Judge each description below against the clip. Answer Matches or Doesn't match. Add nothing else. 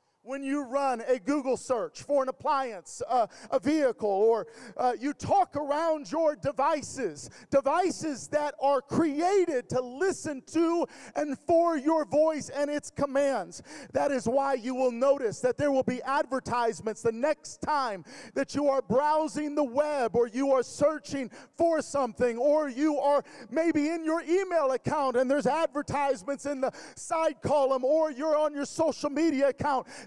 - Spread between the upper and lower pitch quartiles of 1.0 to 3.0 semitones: Matches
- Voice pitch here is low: Doesn't match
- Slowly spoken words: Doesn't match